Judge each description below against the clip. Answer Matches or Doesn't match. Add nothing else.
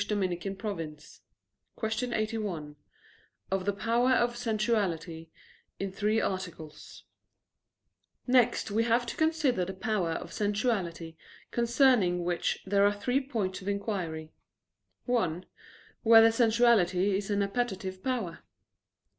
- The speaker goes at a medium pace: Doesn't match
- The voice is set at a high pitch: Matches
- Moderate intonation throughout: Matches